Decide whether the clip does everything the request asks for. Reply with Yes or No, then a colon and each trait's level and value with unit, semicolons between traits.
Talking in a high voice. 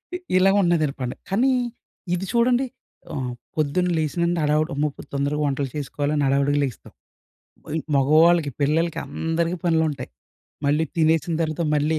No: medium, 155 Hz